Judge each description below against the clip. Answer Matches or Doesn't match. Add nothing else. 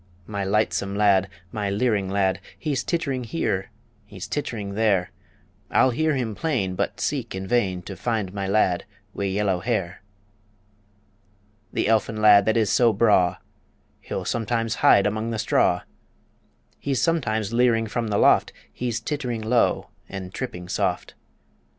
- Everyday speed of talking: Matches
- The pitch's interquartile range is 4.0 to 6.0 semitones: Doesn't match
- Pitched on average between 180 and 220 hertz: Doesn't match